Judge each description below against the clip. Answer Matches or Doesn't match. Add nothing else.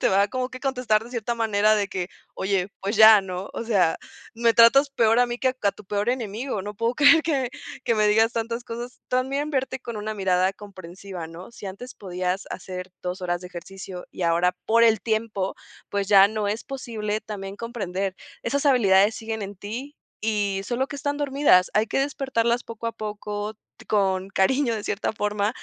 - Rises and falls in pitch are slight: Doesn't match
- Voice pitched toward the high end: Matches